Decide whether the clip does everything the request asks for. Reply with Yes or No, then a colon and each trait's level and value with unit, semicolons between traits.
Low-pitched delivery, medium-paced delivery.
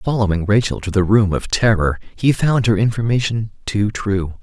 Yes: low, 105 Hz; average, 175 wpm